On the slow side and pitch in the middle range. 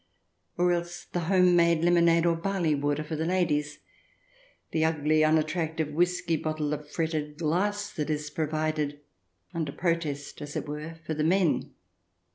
No: average, 150 wpm; medium, 160 Hz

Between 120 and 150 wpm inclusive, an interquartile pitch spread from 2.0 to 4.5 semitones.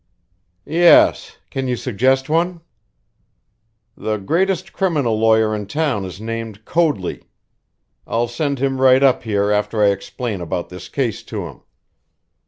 No: slow, 135 wpm; average, 5.2 semitones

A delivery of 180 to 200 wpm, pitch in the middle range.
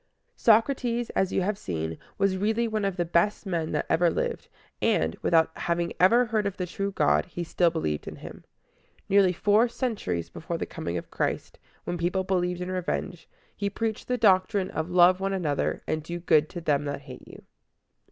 Yes: average, 190 wpm; medium, 180 Hz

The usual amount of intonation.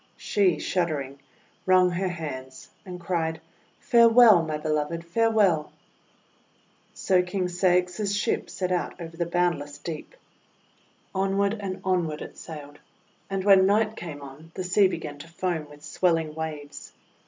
Yes: average, 3.5 semitones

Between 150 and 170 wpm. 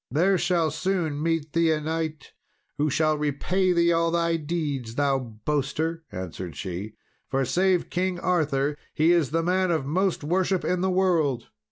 Yes: average, 165 wpm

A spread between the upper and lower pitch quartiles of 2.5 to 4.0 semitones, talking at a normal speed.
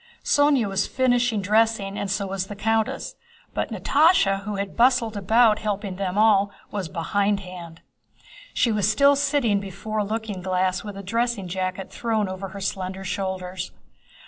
Yes: average, 2.8 semitones; average, 155 wpm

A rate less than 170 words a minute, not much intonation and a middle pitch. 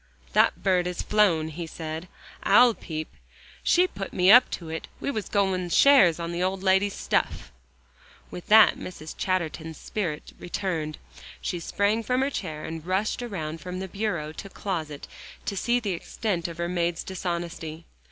No: average, 160 wpm; average, 3.7 semitones; medium, 180 Hz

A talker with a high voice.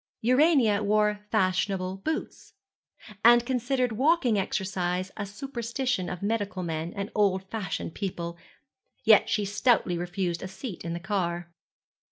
Yes: high, 200 Hz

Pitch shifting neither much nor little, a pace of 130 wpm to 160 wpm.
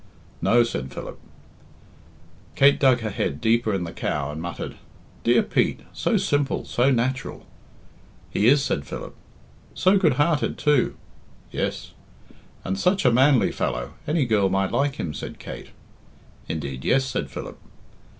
No: wide, 8.0 semitones; average, 145 wpm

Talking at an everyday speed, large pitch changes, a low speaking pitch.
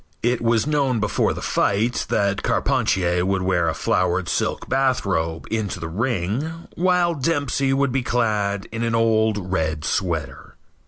Yes: average, 150 wpm; wide, 6.1 semitones; low, 110 Hz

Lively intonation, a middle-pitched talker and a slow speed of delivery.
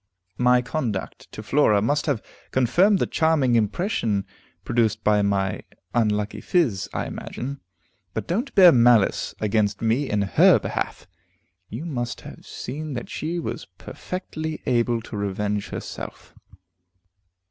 No: wide, 6.4 semitones; low, 120 Hz; slow, 130 wpm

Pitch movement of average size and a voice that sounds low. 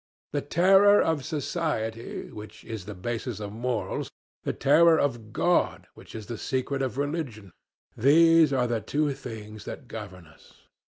No: wide, 5.8 semitones; low, 125 Hz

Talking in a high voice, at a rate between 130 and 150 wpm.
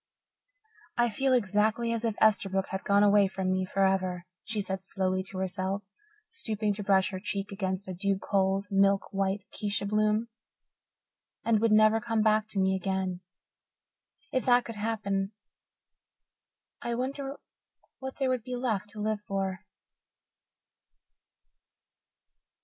Yes: high, 205 Hz; average, 140 wpm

